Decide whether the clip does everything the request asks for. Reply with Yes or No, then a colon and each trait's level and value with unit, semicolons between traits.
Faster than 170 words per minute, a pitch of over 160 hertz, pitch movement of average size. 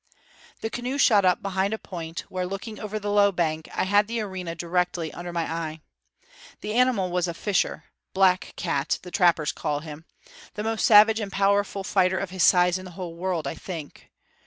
Yes: average, 195 wpm; medium, 185 Hz; average, 3.1 semitones